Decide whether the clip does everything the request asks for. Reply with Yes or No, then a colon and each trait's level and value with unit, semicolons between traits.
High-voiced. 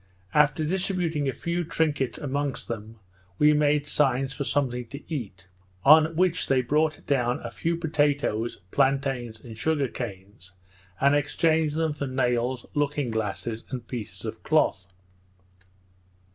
No: medium, 140 Hz